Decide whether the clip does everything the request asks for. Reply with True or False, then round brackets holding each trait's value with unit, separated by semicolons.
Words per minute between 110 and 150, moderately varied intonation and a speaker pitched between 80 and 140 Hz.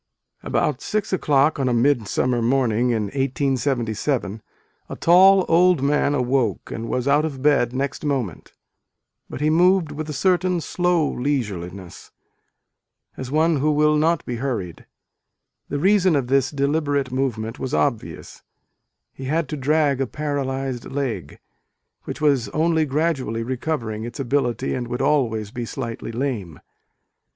True (145 wpm; 4.0 semitones; 135 Hz)